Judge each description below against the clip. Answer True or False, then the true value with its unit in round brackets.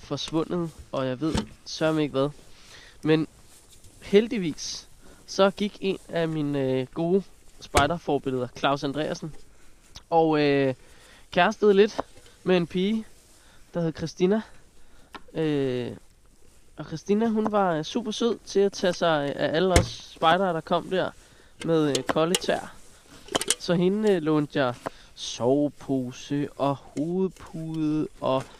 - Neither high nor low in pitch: True (160 Hz)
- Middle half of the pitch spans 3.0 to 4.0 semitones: False (4.7 semitones)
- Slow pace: True (130 wpm)